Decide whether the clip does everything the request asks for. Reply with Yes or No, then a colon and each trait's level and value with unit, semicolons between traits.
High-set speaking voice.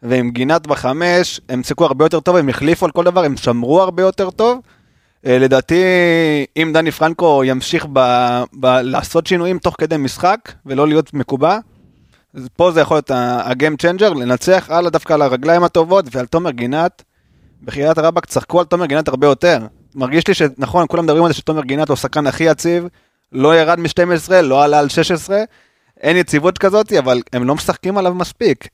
No: medium, 160 Hz